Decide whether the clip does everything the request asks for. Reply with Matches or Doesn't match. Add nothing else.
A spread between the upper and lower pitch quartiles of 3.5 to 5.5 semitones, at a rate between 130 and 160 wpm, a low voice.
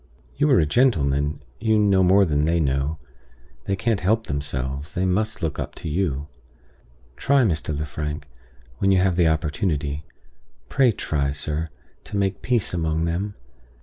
Matches